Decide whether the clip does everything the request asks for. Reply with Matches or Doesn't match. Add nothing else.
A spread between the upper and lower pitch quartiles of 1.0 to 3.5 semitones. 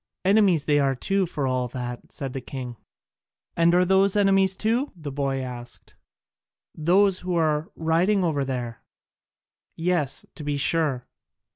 Doesn't match